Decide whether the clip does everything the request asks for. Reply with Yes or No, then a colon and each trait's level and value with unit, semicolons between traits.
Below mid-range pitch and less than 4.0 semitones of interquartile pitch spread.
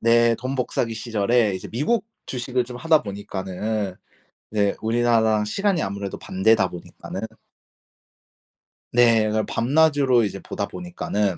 Yes: low, 115 Hz; average, 3.6 semitones